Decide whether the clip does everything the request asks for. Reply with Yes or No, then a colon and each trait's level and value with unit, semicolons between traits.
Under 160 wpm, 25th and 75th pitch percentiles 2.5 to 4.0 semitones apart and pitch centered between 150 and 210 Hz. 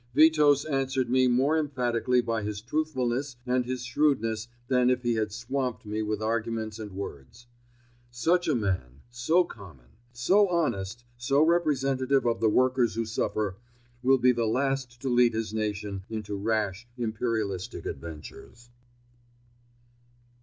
No: average, 140 wpm; average, 3.5 semitones; low, 120 Hz